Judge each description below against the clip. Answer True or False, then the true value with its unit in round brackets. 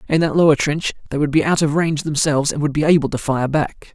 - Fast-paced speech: True (275 wpm)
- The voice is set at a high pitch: False (150 Hz)